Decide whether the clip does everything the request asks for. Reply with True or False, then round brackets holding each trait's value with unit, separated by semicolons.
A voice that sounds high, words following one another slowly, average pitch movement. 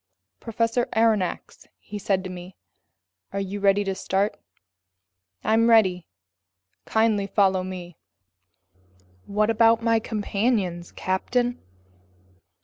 True (205 Hz; 100 wpm; 3.2 semitones)